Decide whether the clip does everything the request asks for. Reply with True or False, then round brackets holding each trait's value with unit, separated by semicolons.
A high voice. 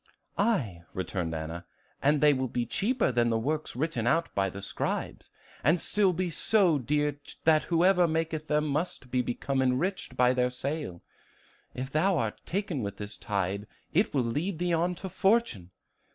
False (145 Hz)